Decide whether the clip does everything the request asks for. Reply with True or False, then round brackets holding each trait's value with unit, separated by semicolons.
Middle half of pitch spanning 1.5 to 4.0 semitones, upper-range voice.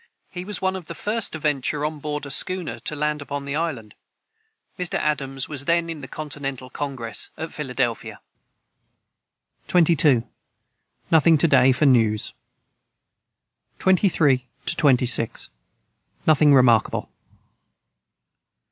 False (3.6 semitones; 145 Hz)